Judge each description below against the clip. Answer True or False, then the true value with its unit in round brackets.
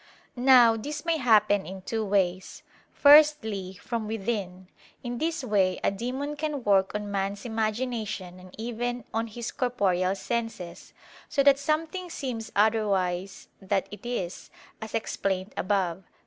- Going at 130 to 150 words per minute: True (140 wpm)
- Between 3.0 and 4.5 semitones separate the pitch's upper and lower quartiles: True (4.2 semitones)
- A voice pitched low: False (220 Hz)